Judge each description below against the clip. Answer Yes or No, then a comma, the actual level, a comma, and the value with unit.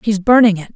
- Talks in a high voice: Yes, high, 205 Hz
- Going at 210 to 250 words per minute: Yes, fast, 240 wpm